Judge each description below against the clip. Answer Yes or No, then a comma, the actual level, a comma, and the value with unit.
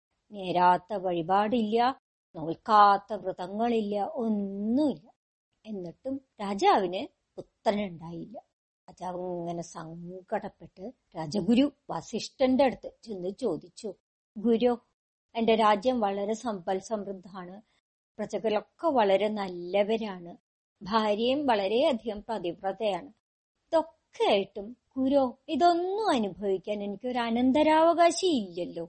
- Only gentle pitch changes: No, average, 4.2 semitones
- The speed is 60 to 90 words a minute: Yes, average, 75 wpm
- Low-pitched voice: No, high, 210 Hz